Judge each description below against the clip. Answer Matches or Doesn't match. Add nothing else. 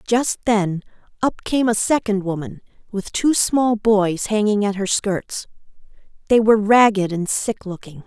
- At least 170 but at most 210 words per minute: Doesn't match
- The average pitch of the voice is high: Matches